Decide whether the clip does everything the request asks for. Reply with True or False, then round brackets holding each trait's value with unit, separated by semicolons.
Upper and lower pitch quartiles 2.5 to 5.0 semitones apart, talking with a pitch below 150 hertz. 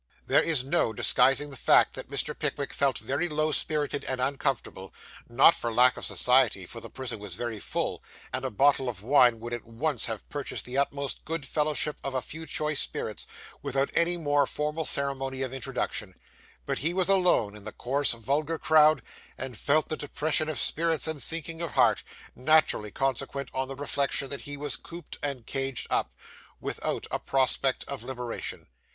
True (3.3 semitones; 140 Hz)